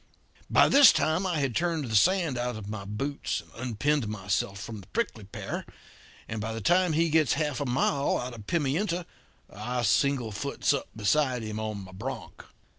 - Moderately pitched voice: No, low, 125 Hz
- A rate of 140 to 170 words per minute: No, average, 185 wpm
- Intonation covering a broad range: Yes, wide, 5.9 semitones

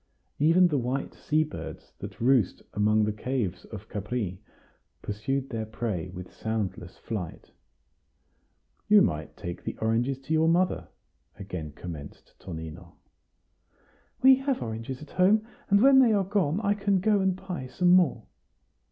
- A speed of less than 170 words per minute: Yes, average, 145 wpm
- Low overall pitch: Yes, low, 130 Hz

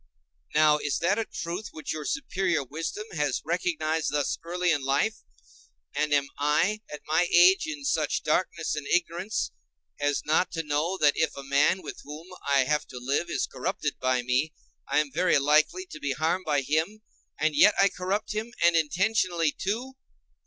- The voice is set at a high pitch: No, medium, 160 Hz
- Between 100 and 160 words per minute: No, average, 180 wpm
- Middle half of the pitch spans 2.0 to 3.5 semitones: No, average, 3.9 semitones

